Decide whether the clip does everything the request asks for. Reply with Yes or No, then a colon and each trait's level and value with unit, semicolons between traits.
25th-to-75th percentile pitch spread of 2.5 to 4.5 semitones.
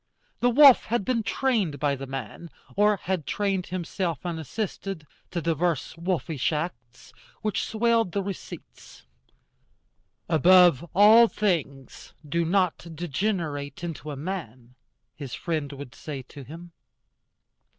No: wide, 5.5 semitones